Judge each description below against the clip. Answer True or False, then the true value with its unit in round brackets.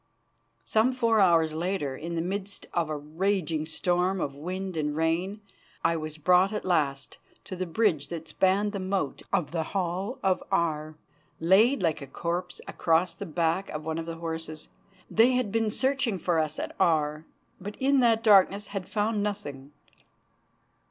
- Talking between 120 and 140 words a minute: False (170 wpm)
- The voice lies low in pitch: False (180 Hz)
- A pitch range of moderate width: True (4.0 semitones)